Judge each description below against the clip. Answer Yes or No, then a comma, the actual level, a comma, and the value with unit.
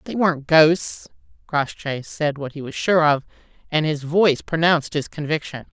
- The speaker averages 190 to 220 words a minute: No, average, 165 wpm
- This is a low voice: No, medium, 155 Hz